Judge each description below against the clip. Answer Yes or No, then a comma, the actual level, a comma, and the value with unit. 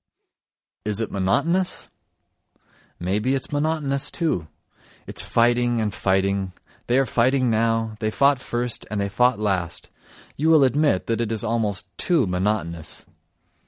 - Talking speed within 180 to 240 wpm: No, slow, 135 wpm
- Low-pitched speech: Yes, low, 115 Hz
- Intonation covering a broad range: No, average, 5.0 semitones